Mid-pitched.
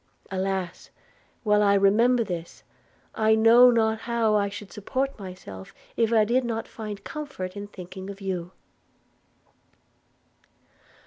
No: high, 210 Hz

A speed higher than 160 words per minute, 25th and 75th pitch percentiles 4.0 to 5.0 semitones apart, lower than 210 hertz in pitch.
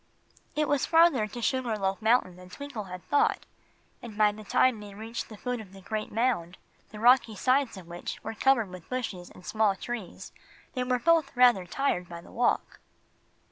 No: average, 190 wpm; average, 4.7 semitones; high, 220 Hz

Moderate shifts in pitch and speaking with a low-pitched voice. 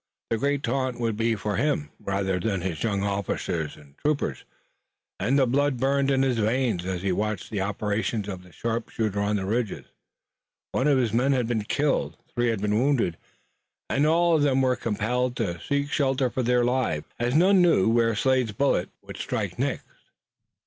Yes: average, 4.7 semitones; low, 115 Hz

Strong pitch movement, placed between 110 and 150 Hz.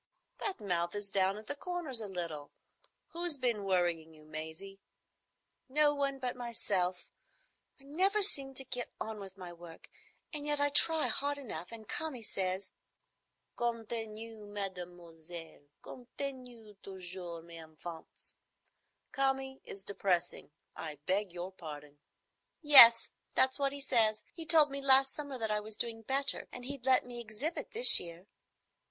No: wide, 7.1 semitones; high, 220 Hz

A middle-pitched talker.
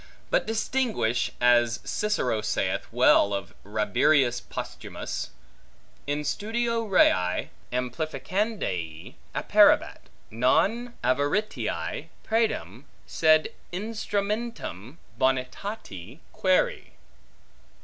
Yes: medium, 150 Hz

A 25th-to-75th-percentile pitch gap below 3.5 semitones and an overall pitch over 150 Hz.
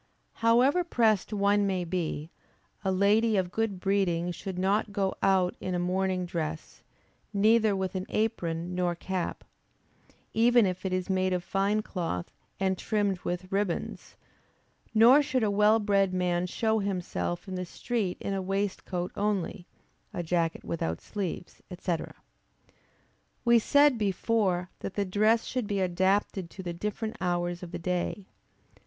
Yes: average, 2.8 semitones; high, 190 Hz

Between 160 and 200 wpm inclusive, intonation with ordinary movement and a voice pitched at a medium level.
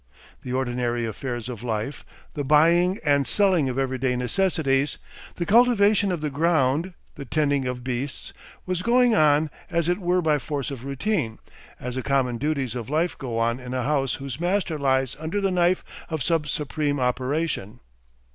Yes: average, 170 wpm; average, 4.9 semitones; medium, 145 Hz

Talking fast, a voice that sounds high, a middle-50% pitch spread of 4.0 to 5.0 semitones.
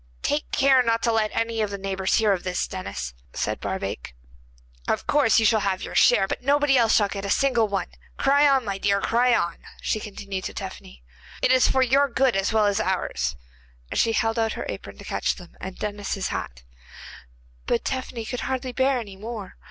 Yes: fast, 210 wpm; high, 220 Hz; average, 4.4 semitones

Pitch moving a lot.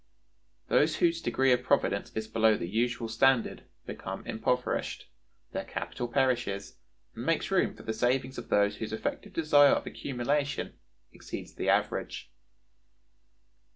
No: average, 3.9 semitones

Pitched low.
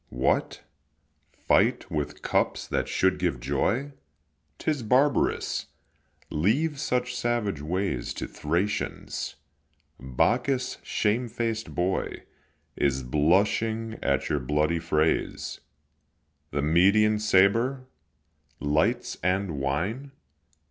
Yes: low, 100 Hz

